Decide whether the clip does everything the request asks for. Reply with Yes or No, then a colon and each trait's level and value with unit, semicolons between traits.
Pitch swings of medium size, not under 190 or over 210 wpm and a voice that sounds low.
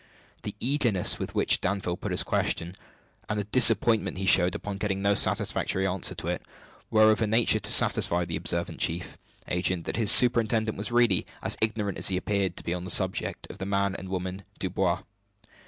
Yes: average, 3.0 semitones; average, 195 wpm; very low, 95 Hz